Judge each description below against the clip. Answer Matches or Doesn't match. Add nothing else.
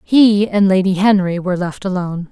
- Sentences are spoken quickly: Doesn't match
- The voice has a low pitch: Doesn't match